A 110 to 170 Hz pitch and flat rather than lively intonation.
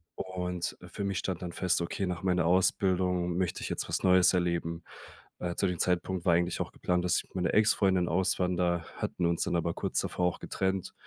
No: very low, 90 Hz; narrow, 1.2 semitones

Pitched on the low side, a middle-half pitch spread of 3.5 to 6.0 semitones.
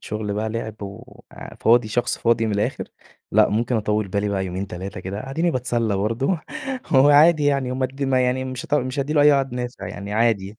Yes: low, 120 Hz; average, 4.2 semitones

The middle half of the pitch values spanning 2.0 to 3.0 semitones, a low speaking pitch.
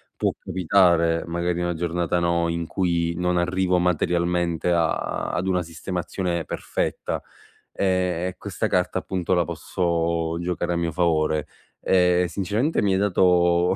No: narrow, 1.3 semitones; very low, 85 Hz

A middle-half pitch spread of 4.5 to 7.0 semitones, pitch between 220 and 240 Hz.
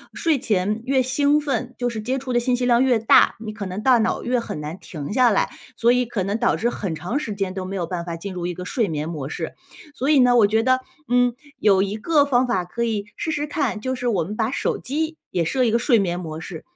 Yes: average, 5.1 semitones; high, 225 Hz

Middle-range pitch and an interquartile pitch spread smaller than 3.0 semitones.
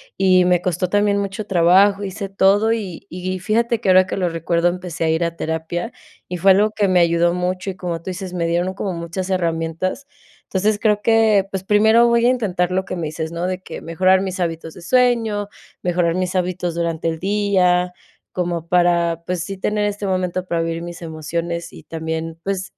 Yes: medium, 180 Hz; narrow, 2.6 semitones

